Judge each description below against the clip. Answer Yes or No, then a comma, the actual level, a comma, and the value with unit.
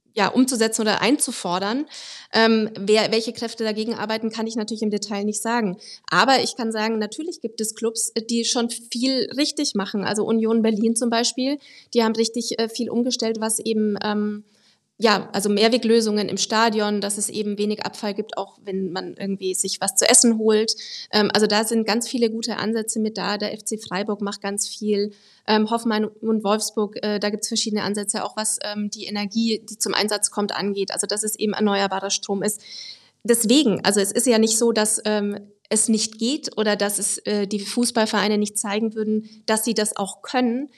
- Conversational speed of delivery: No, fast, 195 wpm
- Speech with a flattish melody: Yes, narrow, 1.7 semitones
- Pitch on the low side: No, high, 215 Hz